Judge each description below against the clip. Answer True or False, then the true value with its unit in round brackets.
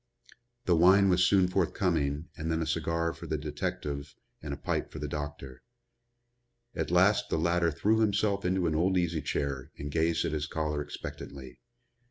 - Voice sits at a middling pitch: False (80 Hz)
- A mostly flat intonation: False (3.6 semitones)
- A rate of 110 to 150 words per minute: False (175 wpm)